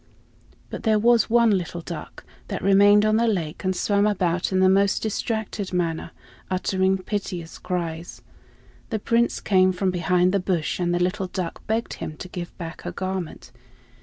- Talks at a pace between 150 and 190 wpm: Yes, average, 170 wpm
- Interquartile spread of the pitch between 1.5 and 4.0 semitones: Yes, narrow, 2.6 semitones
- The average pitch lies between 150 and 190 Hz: Yes, medium, 185 Hz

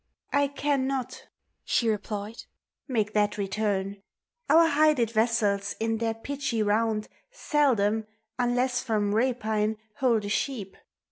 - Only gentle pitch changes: No, average, 3.7 semitones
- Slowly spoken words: Yes, slow, 115 wpm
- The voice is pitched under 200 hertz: No, high, 225 Hz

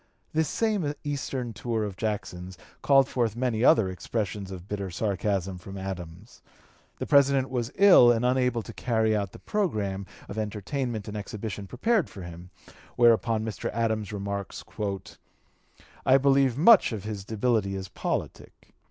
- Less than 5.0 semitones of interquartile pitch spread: Yes, average, 4.5 semitones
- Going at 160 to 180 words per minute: No, average, 145 wpm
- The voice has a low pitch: Yes, low, 110 Hz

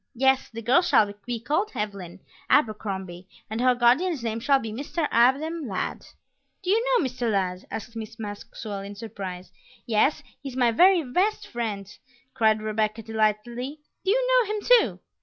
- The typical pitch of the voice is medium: No, high, 235 Hz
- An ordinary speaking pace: Yes, average, 160 wpm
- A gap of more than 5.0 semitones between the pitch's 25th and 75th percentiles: Yes, wide, 5.4 semitones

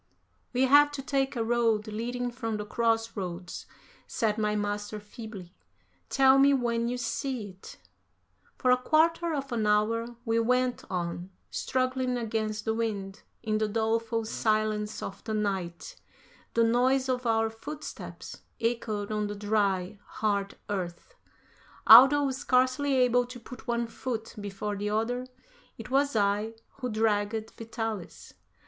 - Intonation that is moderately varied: Yes, average, 3.0 semitones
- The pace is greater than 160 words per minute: No, average, 140 wpm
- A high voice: Yes, high, 225 Hz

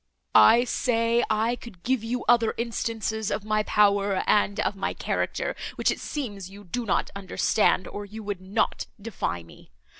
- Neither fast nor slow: Yes, average, 170 wpm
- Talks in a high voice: Yes, high, 215 Hz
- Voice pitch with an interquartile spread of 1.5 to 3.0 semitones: Yes, narrow, 2.5 semitones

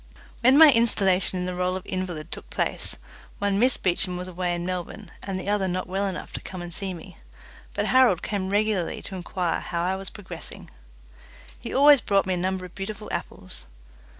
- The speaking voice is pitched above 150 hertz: Yes, high, 190 Hz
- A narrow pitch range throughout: Yes, narrow, 2.0 semitones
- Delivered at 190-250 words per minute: Yes, average, 200 wpm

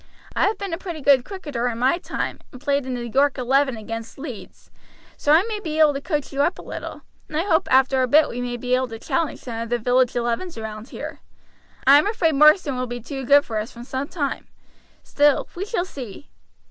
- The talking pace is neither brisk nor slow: No, fast, 235 wpm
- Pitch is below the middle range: No, very high, 270 Hz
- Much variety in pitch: No, average, 4.1 semitones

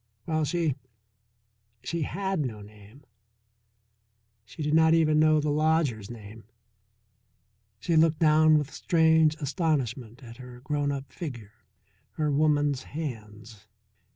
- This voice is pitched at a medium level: Yes, medium, 145 Hz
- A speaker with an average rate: No, slow, 120 wpm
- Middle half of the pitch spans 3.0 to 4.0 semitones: No, average, 4.4 semitones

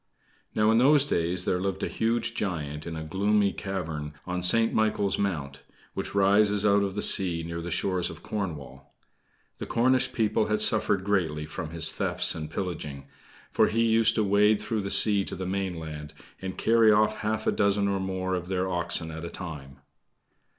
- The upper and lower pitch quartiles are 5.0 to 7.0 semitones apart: No, average, 4.2 semitones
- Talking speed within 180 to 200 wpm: Yes, average, 185 wpm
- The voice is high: No, very low, 95 Hz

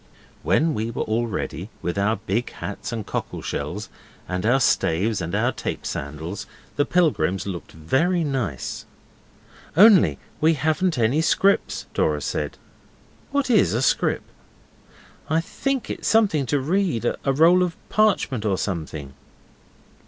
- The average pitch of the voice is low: Yes, low, 120 Hz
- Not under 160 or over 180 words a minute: No, average, 140 wpm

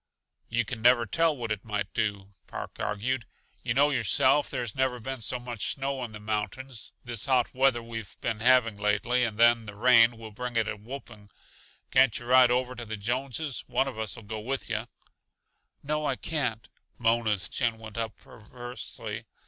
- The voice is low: Yes, low, 120 Hz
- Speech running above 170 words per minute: Yes, average, 180 wpm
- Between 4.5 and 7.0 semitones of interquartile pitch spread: No, average, 2.8 semitones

